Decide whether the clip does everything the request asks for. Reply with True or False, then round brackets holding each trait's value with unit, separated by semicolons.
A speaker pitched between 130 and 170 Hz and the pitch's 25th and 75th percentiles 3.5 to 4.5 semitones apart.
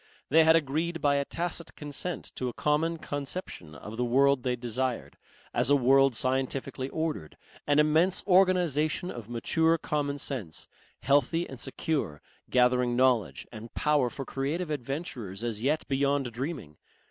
True (140 Hz; 4.1 semitones)